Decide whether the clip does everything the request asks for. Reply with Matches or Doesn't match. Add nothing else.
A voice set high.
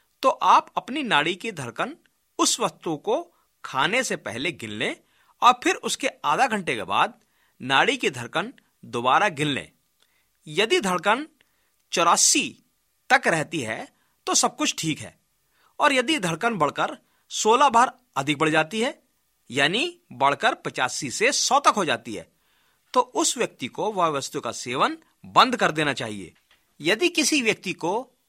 Matches